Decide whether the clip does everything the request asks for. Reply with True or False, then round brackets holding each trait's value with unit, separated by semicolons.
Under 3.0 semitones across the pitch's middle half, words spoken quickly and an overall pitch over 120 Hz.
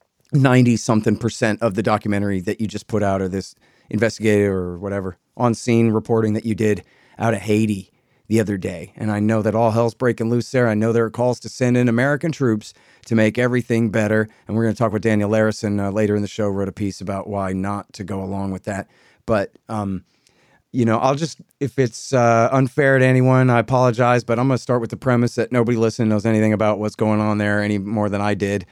False (2.6 semitones; 235 wpm; 110 Hz)